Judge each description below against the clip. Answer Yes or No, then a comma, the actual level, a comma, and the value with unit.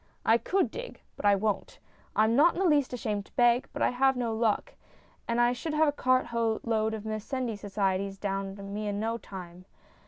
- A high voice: Yes, high, 225 Hz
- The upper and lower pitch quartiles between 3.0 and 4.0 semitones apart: Yes, average, 3.6 semitones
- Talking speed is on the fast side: Yes, fast, 215 wpm